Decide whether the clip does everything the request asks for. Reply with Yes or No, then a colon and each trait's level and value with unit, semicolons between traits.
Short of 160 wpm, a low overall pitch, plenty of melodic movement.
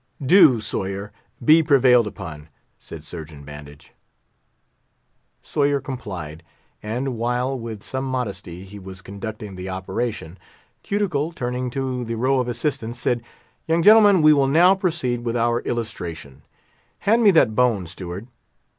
Yes: slow, 135 wpm; low, 120 Hz; wide, 6.1 semitones